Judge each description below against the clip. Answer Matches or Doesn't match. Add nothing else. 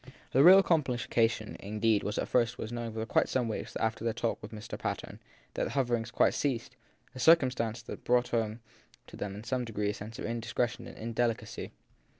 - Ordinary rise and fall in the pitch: Doesn't match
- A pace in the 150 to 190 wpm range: Matches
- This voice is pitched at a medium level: Doesn't match